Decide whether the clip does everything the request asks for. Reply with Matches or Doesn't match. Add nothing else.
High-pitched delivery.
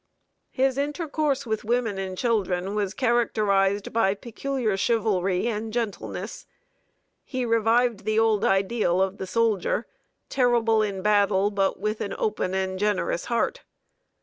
Matches